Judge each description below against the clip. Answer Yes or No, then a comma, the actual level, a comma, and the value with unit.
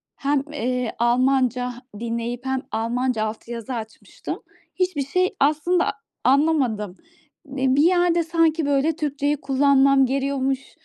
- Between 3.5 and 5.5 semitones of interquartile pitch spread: No, average, 3.1 semitones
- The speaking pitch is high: Yes, very high, 270 Hz